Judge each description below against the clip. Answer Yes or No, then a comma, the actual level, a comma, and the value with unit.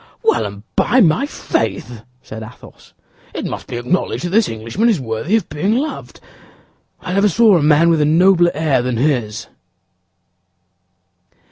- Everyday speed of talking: Yes, average, 155 wpm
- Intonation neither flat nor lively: No, wide, 8.4 semitones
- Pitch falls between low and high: Yes, medium, 155 Hz